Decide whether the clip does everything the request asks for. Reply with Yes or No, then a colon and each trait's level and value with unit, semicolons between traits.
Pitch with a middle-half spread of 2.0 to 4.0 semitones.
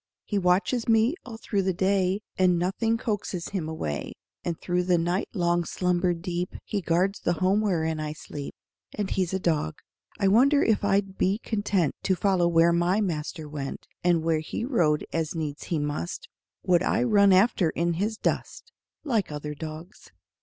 Yes: average, 3.4 semitones